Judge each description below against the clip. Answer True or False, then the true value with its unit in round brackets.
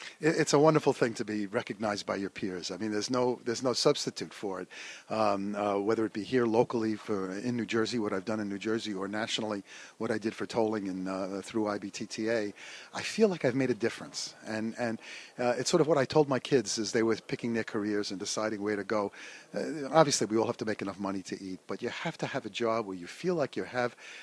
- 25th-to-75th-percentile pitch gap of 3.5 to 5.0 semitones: False (3.1 semitones)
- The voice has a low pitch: True (110 Hz)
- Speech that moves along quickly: True (250 wpm)